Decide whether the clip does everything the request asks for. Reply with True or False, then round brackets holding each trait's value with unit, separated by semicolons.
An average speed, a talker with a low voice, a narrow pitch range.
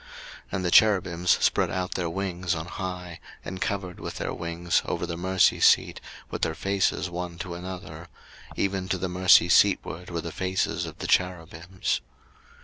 True (170 wpm; 90 Hz; 1.4 semitones)